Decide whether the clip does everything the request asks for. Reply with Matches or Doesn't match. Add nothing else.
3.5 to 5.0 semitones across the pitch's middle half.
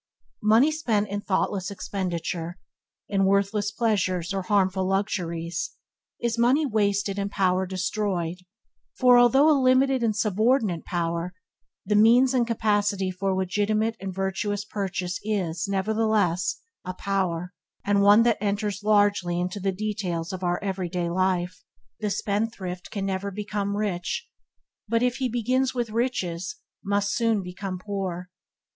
Doesn't match